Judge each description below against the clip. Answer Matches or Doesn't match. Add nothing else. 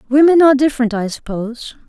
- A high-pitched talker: Matches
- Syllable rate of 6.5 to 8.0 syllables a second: Matches